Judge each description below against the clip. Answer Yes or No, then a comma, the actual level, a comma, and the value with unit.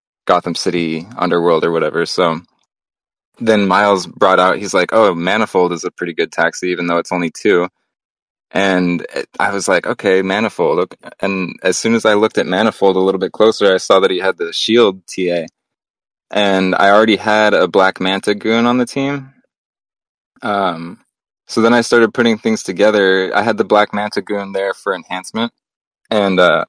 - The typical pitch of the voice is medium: No, low, 100 Hz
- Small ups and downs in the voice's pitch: No, average, 3.1 semitones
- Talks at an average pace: Yes, average, 185 wpm